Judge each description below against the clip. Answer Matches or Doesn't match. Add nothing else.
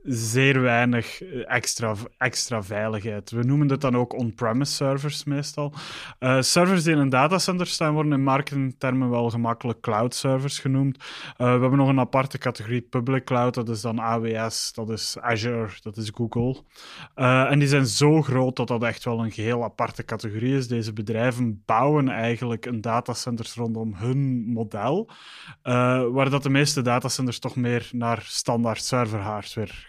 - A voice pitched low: Matches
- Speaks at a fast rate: Doesn't match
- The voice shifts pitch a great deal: Doesn't match